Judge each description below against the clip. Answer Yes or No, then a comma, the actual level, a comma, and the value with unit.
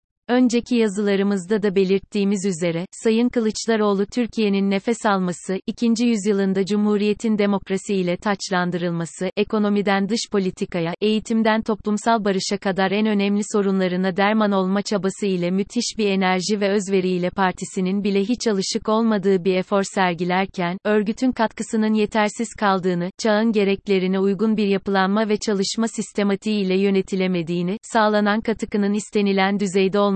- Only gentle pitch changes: Yes, narrow, 2.1 semitones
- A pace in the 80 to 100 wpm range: No, average, 125 wpm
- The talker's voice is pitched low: No, high, 205 Hz